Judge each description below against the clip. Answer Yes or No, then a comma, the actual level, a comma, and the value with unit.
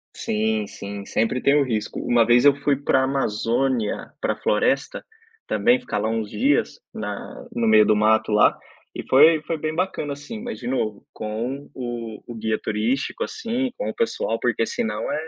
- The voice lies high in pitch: No, low, 130 Hz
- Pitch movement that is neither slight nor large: No, wide, 6.3 semitones